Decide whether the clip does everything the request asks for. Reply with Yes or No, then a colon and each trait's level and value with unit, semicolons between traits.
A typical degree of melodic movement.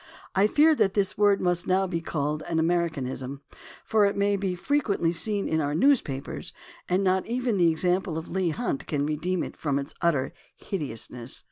Yes: average, 4.5 semitones